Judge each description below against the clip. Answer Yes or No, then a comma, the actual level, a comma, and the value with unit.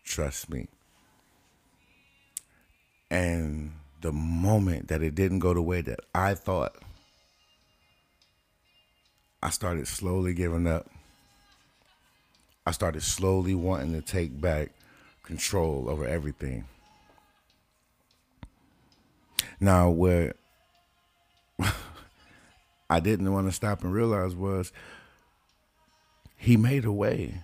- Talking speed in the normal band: No, slow, 95 wpm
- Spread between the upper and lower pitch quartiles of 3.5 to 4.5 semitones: No, average, 2.8 semitones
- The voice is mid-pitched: No, very low, 90 Hz